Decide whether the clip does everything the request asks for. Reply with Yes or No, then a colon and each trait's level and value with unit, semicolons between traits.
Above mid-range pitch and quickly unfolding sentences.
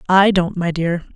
No: medium, 180 Hz; fast, 210 wpm